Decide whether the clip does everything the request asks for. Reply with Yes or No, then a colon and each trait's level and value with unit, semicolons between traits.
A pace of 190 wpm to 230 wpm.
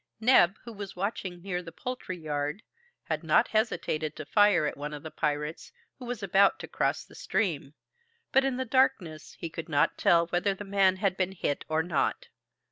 Yes: average, 195 wpm